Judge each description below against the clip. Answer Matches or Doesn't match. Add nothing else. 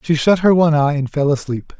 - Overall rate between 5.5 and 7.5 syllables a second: Matches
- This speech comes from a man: Matches